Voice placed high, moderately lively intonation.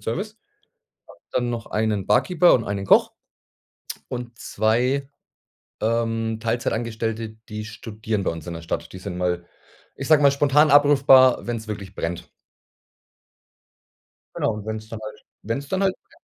No: low, 115 Hz; average, 3.7 semitones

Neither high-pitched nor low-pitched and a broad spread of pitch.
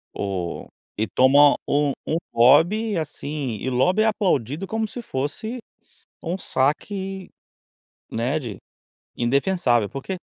Yes: medium, 145 Hz; wide, 7.3 semitones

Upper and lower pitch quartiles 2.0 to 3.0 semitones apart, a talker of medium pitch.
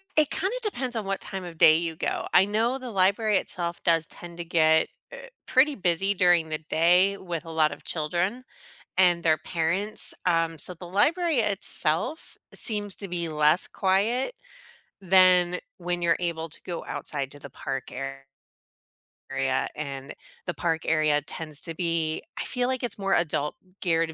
No: average, 3.7 semitones; medium, 175 Hz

